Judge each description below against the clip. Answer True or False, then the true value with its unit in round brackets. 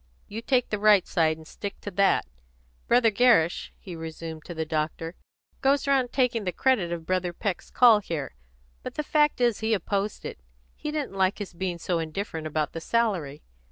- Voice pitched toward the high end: True (195 Hz)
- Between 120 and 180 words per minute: False (190 wpm)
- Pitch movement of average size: False (6.0 semitones)